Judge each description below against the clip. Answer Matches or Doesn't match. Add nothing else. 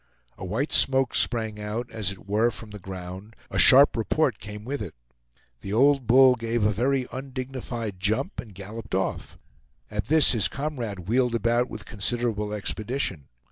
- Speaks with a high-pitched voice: Doesn't match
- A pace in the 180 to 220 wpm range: Doesn't match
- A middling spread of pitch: Matches